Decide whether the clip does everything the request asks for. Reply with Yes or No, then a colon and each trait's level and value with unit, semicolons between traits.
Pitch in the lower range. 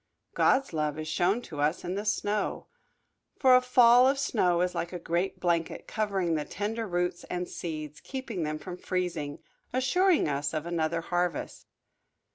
No: medium, 180 Hz